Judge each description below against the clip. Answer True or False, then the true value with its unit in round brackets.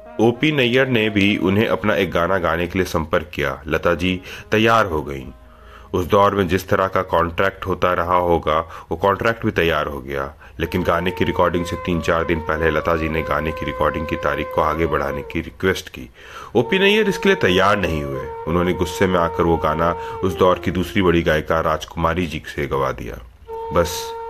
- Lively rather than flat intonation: False (3.9 semitones)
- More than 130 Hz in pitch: False (90 Hz)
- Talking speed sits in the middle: False (205 wpm)